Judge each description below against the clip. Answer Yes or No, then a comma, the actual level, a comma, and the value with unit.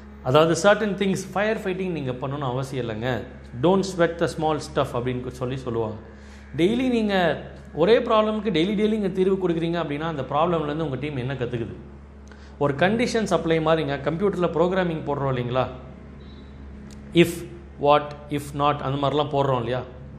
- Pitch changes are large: Yes, wide, 5.8 semitones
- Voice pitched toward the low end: No, medium, 145 Hz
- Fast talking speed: Yes, fast, 145 wpm